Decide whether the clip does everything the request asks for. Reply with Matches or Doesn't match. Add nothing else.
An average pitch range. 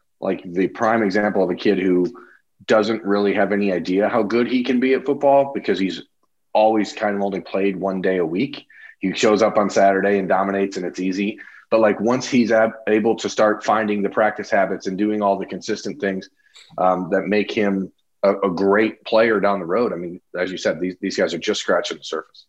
Doesn't match